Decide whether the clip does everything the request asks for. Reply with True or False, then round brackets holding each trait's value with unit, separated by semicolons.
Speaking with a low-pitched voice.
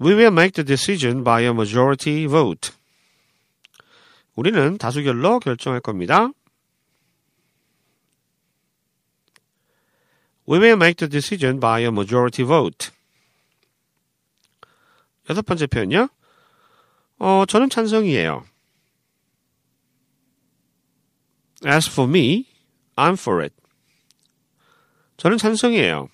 False (155 Hz)